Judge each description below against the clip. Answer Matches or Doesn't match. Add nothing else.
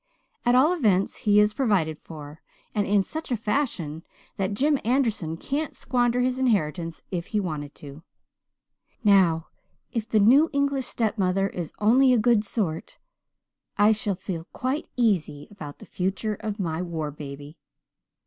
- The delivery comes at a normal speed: Matches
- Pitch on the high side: Matches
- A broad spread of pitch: Matches